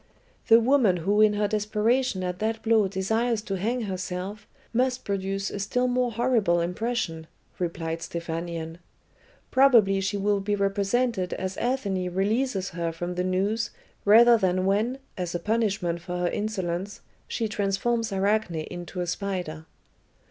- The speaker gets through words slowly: No, average, 145 wpm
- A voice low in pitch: No, high, 200 Hz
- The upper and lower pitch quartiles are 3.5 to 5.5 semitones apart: Yes, average, 3.8 semitones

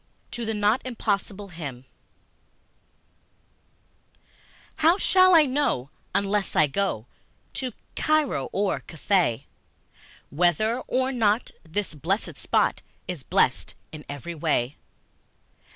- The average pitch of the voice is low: No, high, 200 Hz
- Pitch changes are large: Yes, wide, 7.8 semitones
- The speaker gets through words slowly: Yes, slow, 105 wpm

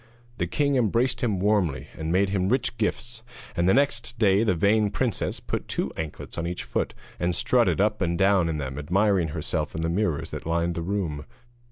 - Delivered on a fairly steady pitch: No, average, 4.5 semitones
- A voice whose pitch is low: Yes, very low, 95 Hz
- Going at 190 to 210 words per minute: Yes, average, 200 wpm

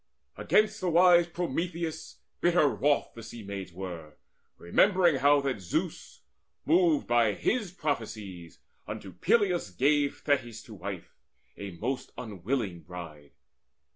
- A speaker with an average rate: No, slow, 120 wpm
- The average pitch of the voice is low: Yes, low, 125 Hz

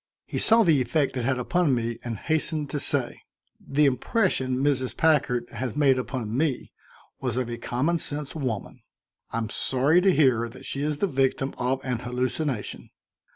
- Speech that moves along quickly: No, average, 170 wpm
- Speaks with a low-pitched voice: Yes, low, 130 Hz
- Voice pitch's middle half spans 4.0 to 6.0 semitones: No, average, 3.5 semitones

